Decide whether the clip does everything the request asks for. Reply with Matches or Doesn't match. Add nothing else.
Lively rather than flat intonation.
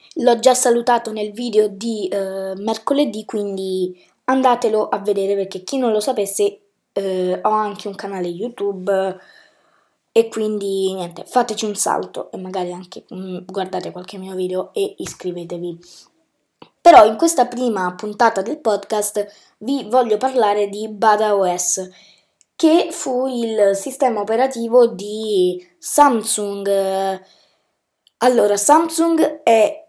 Doesn't match